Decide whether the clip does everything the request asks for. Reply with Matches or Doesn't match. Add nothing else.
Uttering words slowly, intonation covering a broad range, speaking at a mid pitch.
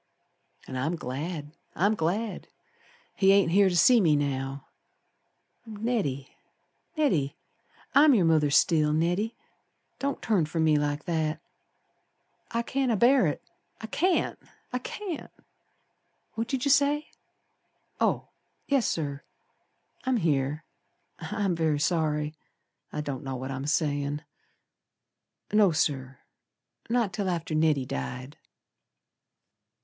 Matches